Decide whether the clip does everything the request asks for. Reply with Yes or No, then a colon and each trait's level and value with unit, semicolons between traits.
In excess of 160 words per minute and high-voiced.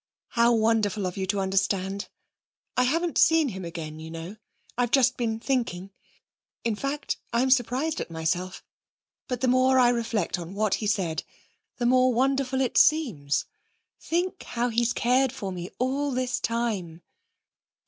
No: average, 155 wpm; high, 235 Hz